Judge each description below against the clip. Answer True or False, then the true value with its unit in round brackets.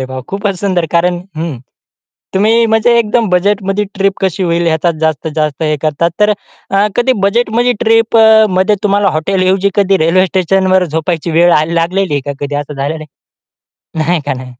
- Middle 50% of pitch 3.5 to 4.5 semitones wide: True (4.2 semitones)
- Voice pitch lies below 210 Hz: True (185 Hz)